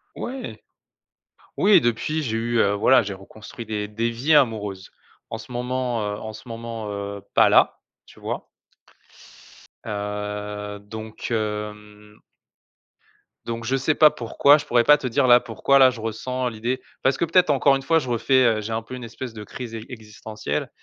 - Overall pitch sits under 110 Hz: No, low, 115 Hz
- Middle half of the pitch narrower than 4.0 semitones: Yes, average, 3.4 semitones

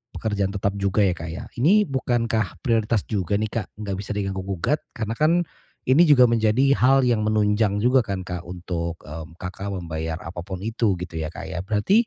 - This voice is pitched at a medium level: No, low, 100 Hz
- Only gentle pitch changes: No, average, 4.3 semitones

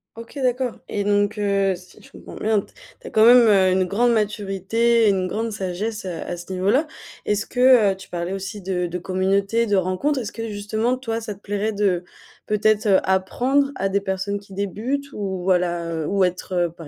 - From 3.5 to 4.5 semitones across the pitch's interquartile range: No, average, 3.1 semitones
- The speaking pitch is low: No, high, 200 Hz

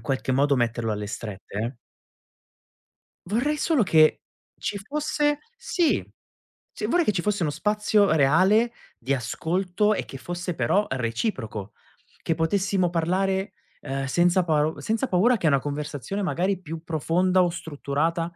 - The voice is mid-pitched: Yes, medium, 175 Hz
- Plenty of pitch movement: Yes, wide, 6.3 semitones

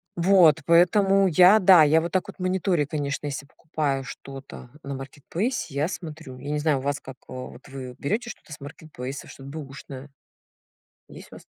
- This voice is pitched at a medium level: Yes, medium, 150 Hz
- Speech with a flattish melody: No, average, 4.3 semitones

